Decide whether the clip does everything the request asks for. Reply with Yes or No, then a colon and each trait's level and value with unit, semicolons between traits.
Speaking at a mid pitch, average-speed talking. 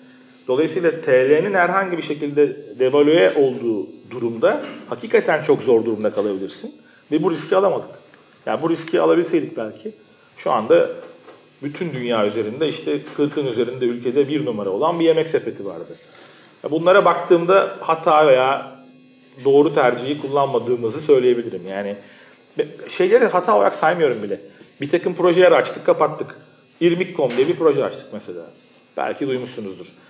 Yes: medium, 170 Hz; average, 130 wpm